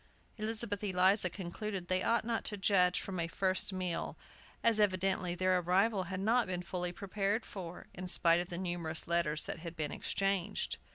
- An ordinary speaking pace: Yes, average, 175 wpm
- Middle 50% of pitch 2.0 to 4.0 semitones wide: Yes, narrow, 2.4 semitones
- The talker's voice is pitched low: No, medium, 185 Hz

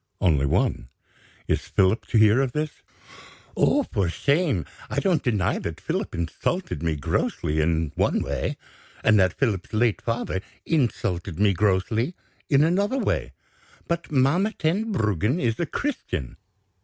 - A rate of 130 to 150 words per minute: Yes, average, 140 wpm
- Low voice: Yes, low, 115 Hz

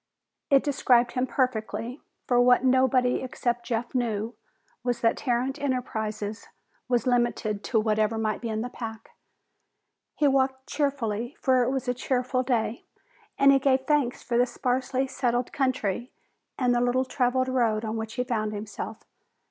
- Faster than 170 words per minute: No, average, 155 wpm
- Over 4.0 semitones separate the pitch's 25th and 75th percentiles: No, narrow, 2.4 semitones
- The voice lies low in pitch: No, high, 245 Hz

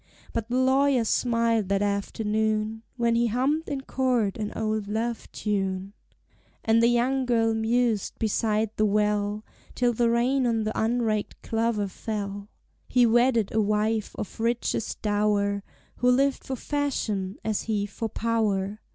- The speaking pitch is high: Yes, high, 220 Hz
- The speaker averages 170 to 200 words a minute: No, average, 145 wpm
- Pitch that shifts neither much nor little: No, narrow, 2.3 semitones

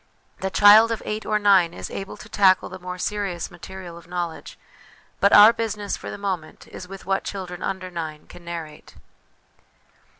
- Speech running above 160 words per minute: Yes, average, 175 wpm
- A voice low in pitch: No, high, 190 Hz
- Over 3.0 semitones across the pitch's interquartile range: No, average, 2.7 semitones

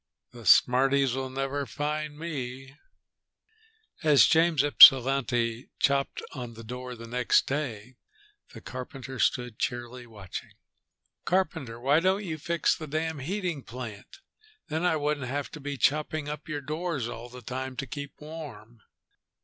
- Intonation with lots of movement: No, average, 3.6 semitones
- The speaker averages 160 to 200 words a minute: No, slow, 135 wpm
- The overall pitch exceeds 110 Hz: Yes, low, 135 Hz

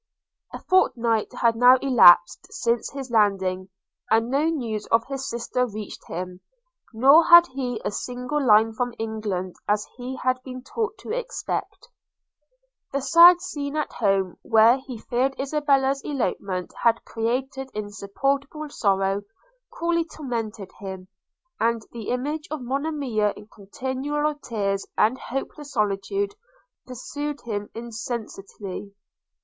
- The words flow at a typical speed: No, slow, 125 wpm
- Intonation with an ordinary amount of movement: Yes, average, 4.7 semitones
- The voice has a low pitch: No, high, 245 Hz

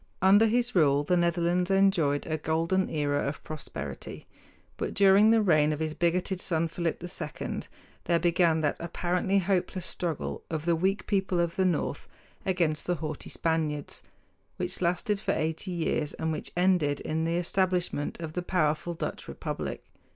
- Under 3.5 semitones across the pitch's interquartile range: Yes, average, 2.8 semitones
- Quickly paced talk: No, average, 160 wpm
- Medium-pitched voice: Yes, medium, 170 Hz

